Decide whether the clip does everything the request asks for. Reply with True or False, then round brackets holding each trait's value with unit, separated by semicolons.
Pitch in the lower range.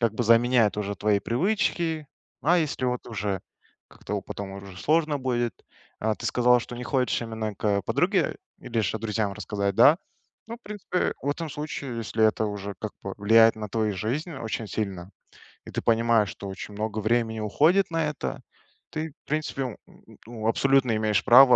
True (115 Hz)